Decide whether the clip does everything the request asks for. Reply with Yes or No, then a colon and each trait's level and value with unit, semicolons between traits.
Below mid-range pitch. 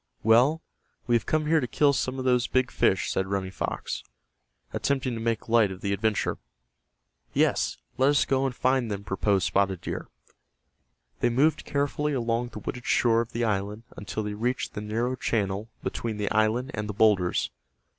Yes: low, 115 Hz